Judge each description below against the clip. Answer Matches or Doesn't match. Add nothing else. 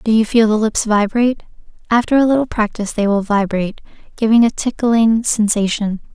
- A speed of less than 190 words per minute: Matches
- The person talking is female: Matches